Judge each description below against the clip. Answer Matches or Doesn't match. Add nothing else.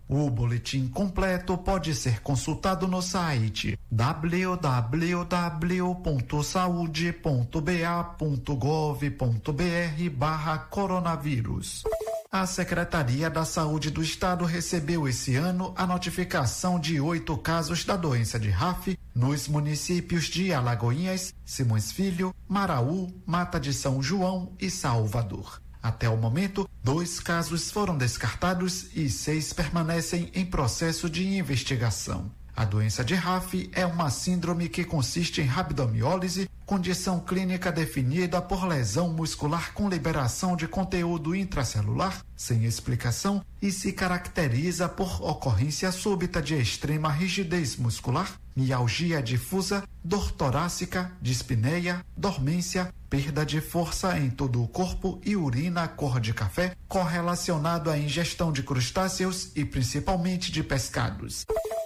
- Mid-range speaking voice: Matches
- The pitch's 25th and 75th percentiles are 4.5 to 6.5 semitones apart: Matches